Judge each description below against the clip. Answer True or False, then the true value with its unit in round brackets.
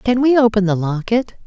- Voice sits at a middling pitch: False (220 Hz)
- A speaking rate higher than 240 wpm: False (205 wpm)